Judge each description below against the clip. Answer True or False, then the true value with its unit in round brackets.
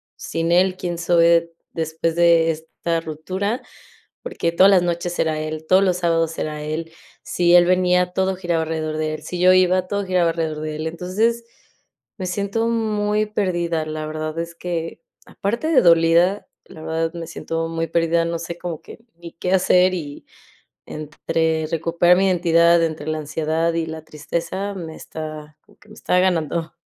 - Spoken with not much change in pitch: True (2.2 semitones)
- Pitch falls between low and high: True (170 Hz)